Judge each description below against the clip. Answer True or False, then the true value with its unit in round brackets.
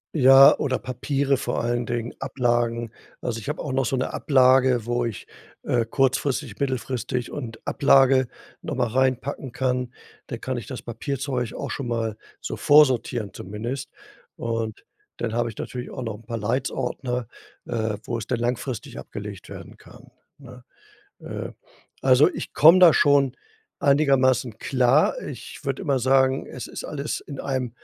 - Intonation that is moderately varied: False (2.2 semitones)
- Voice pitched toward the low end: True (125 Hz)